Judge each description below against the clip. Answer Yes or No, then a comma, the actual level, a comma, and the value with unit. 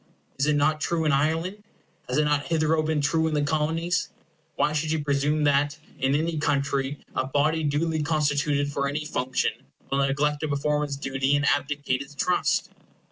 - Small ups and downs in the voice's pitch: Yes, narrow, 1.7 semitones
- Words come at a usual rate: Yes, average, 185 wpm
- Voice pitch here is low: No, medium, 150 Hz